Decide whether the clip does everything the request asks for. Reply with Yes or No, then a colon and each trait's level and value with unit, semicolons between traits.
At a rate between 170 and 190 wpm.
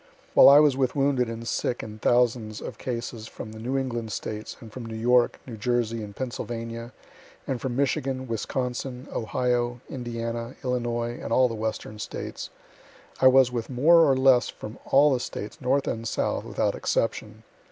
Yes: average, 175 wpm